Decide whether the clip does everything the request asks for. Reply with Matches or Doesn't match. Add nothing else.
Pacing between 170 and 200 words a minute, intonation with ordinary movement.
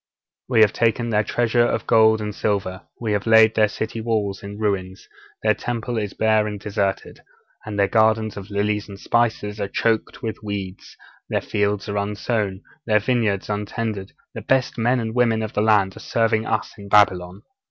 Doesn't match